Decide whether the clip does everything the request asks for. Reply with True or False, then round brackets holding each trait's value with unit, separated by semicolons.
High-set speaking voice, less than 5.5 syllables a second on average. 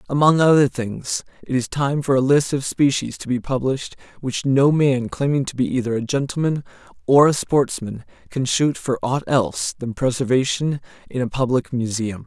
False (135 Hz; 5.0 syllables/s)